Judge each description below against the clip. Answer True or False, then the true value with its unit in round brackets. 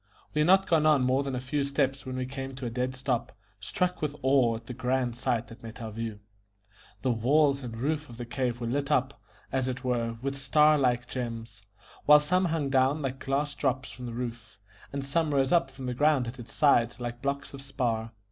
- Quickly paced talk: True (225 wpm)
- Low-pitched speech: True (130 Hz)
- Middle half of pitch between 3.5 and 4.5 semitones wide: False (2.7 semitones)